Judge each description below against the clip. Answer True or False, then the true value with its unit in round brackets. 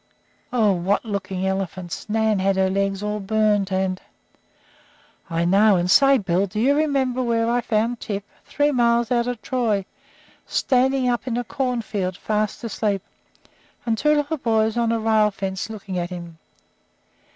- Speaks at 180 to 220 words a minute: False (165 wpm)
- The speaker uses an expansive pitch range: False (3.8 semitones)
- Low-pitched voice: False (215 Hz)